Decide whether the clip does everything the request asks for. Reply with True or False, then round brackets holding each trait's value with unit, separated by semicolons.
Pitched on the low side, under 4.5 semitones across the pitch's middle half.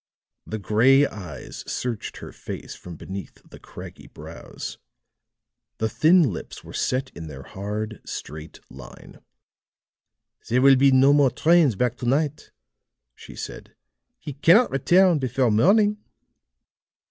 False (130 Hz; 5.6 semitones)